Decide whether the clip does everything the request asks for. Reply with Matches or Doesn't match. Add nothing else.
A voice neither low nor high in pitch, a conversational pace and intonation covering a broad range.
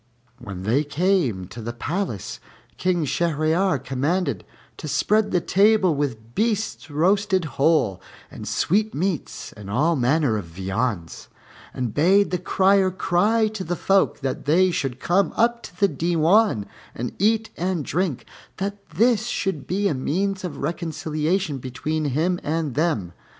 Matches